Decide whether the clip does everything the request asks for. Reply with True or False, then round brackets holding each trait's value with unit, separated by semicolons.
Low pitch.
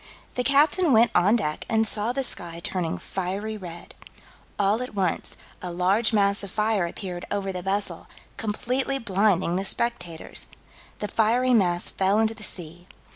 False (205 Hz)